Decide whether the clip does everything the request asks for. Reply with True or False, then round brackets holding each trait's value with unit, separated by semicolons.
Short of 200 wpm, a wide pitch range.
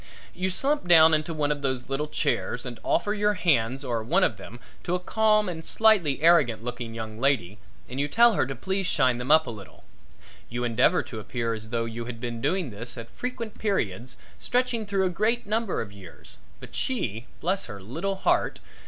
False (205 wpm; 8.6 semitones)